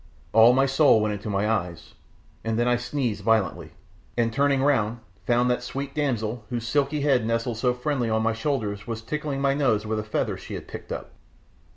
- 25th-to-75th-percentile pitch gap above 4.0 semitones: No, average, 3.7 semitones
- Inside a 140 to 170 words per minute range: No, average, 200 wpm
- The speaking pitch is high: No, low, 120 Hz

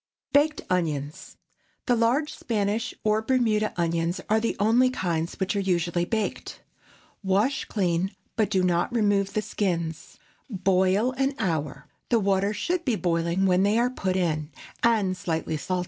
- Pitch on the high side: Yes, high, 195 Hz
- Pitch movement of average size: Yes, average, 4.3 semitones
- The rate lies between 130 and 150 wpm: Yes, average, 145 wpm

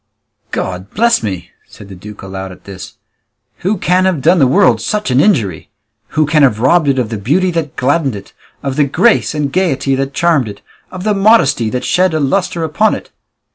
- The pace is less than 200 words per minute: No, fast, 205 wpm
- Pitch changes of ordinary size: No, wide, 8.0 semitones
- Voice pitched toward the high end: No, medium, 140 Hz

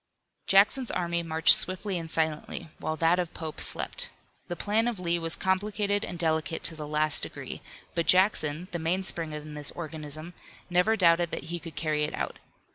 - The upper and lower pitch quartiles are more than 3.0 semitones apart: No, average, 2.7 semitones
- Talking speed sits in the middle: Yes, average, 180 wpm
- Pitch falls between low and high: Yes, medium, 170 Hz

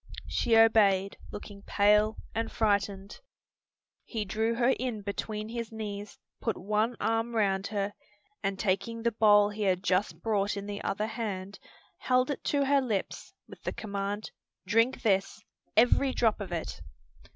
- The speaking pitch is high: Yes, high, 210 Hz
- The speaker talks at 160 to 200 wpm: No, average, 150 wpm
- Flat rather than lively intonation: Yes, narrow, 2.2 semitones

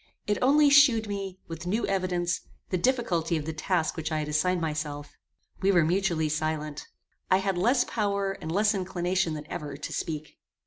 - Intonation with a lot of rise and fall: No, average, 4.1 semitones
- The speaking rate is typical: Yes, average, 180 wpm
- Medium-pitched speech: Yes, medium, 180 Hz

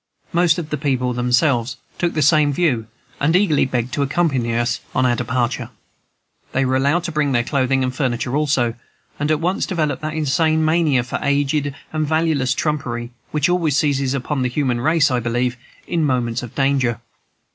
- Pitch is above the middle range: No, medium, 140 Hz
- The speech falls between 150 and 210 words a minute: Yes, average, 180 wpm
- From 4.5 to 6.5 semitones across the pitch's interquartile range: No, average, 3.6 semitones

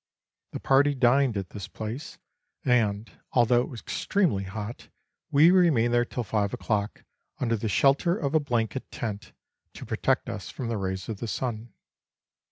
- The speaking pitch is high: No, low, 120 Hz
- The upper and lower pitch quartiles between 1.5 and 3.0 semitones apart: No, average, 4.2 semitones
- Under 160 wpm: No, average, 165 wpm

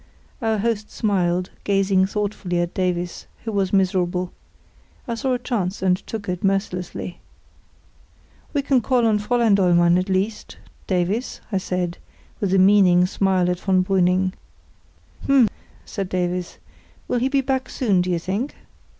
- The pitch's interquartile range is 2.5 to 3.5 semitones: Yes, average, 3.1 semitones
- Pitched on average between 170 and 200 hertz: Yes, high, 190 Hz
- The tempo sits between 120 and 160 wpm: Yes, average, 150 wpm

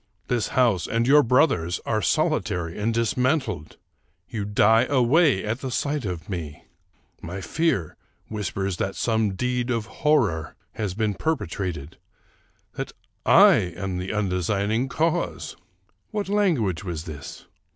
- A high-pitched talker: No, low, 110 Hz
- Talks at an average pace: No, slow, 130 wpm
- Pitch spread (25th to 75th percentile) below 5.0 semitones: No, wide, 5.5 semitones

